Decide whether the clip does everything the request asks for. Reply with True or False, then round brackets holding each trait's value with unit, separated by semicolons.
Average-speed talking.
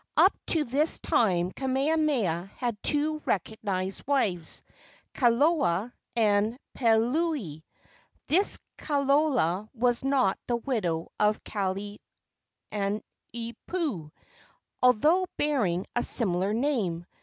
False (85 wpm)